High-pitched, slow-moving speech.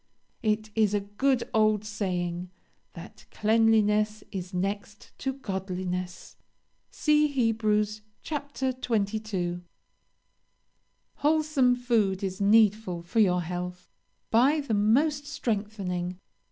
Yes: high, 210 Hz; slow, 100 wpm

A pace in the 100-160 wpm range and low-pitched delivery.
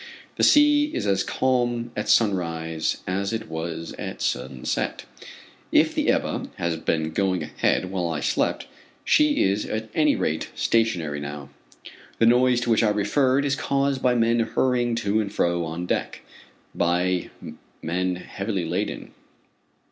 Yes: average, 150 wpm; low, 100 Hz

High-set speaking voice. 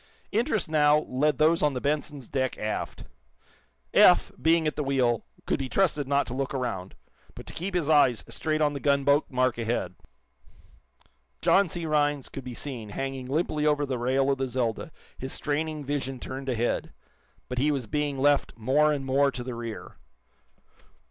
No: medium, 140 Hz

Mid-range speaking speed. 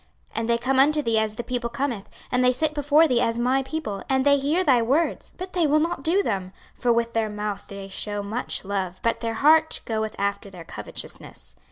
No: fast, 225 wpm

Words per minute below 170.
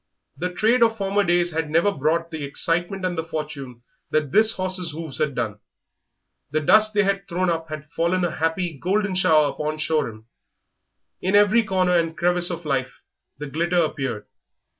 No: average, 175 wpm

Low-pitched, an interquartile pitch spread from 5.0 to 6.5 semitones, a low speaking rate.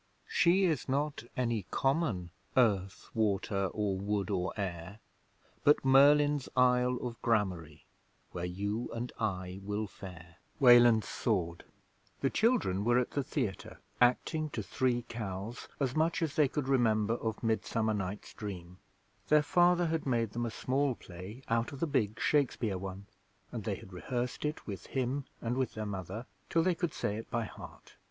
No: low, 115 Hz; average, 5.3 semitones; average, 160 wpm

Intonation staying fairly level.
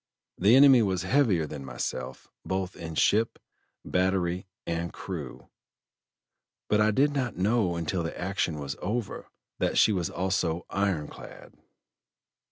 No: average, 4.1 semitones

